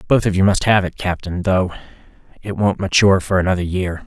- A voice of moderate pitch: No, very low, 95 Hz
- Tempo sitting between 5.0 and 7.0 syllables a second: Yes, 5.9 syllables/s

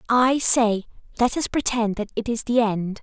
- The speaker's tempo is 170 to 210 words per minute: Yes, average, 200 wpm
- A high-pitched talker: Yes, high, 230 Hz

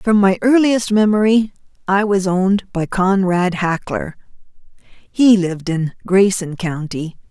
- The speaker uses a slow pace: Yes, slow, 125 wpm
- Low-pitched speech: No, high, 190 Hz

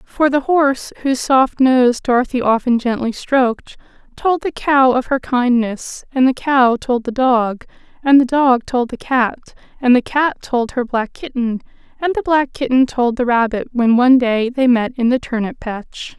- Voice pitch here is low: No, very high, 255 Hz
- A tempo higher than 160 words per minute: Yes, average, 190 wpm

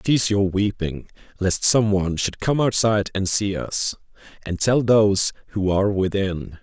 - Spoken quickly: No, average, 165 wpm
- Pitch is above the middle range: No, low, 100 Hz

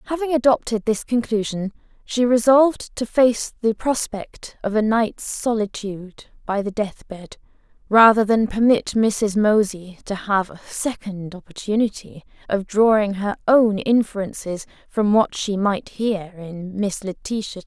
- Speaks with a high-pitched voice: Yes, high, 215 Hz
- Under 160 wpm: Yes, average, 140 wpm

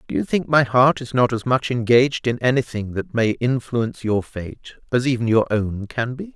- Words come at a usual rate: No, fast, 215 wpm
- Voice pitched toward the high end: No, low, 120 Hz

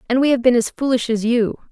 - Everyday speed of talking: No, fast, 280 wpm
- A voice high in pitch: Yes, high, 245 Hz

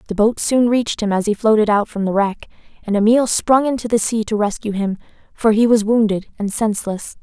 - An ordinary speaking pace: No, fast, 225 wpm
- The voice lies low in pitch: No, high, 215 Hz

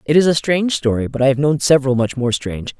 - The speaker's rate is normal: No, fast, 280 wpm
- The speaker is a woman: Yes, female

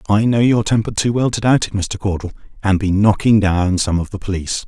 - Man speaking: Yes, male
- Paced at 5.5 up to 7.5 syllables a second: Yes, 5.8 syllables/s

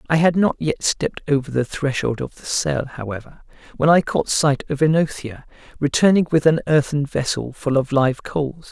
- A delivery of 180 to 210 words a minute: Yes, average, 185 wpm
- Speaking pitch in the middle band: Yes, medium, 145 Hz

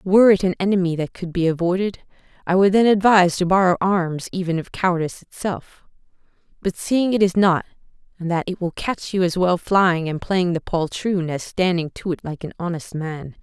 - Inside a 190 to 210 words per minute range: Yes, average, 195 wpm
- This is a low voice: No, medium, 180 Hz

